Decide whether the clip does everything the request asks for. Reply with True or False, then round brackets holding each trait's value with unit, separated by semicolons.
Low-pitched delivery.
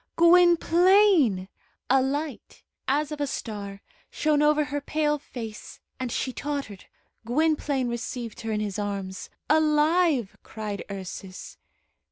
False (275 Hz)